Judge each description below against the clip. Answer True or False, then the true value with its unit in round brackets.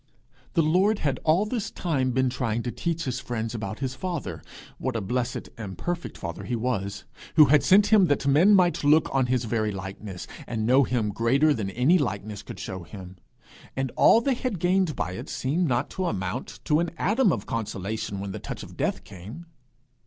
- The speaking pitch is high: False (130 Hz)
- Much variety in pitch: True (7.5 semitones)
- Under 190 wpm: False (200 wpm)